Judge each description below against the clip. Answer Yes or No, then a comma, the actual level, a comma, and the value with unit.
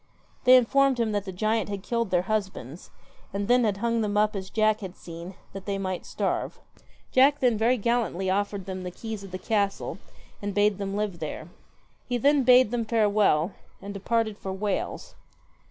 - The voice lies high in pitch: Yes, high, 205 Hz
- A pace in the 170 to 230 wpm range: Yes, average, 185 wpm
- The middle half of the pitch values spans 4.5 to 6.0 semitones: No, average, 3.2 semitones